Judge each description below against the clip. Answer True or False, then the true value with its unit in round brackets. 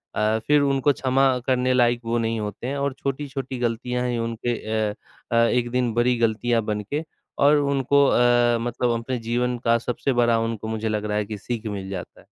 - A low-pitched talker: True (120 Hz)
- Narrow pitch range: True (2.1 semitones)